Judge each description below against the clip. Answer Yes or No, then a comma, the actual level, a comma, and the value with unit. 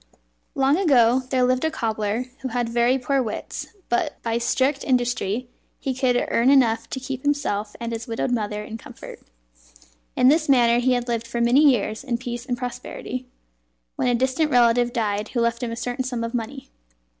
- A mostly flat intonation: Yes, narrow, 2.1 semitones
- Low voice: No, high, 245 Hz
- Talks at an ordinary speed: Yes, average, 190 wpm